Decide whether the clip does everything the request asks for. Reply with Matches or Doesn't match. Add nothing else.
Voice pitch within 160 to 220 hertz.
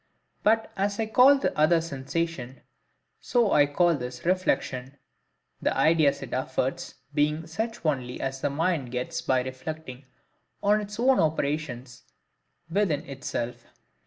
Doesn't match